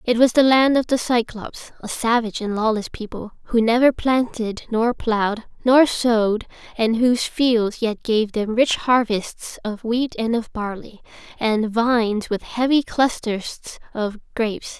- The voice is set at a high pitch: Yes, high, 230 Hz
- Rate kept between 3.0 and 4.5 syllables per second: Yes, 4.3 syllables/s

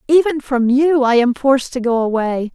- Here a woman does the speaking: Yes, female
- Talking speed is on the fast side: Yes, fast, 210 wpm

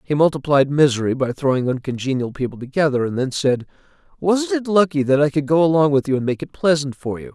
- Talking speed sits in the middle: No, fast, 220 wpm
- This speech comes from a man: Yes, male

